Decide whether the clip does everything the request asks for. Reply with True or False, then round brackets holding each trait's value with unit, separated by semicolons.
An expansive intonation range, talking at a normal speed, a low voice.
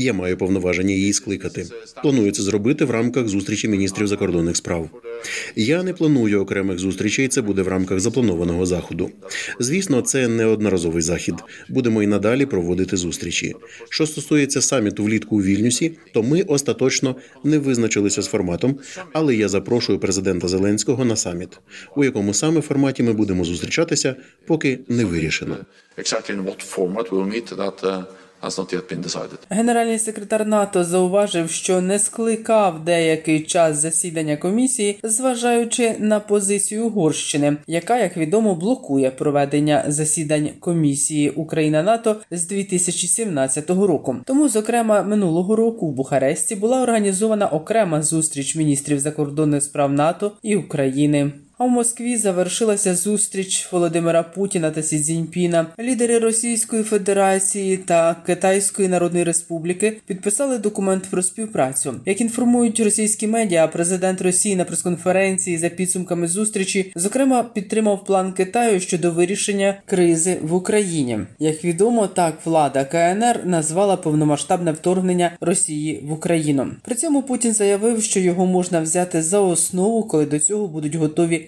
False (7.0 semitones; 130 wpm; 165 Hz)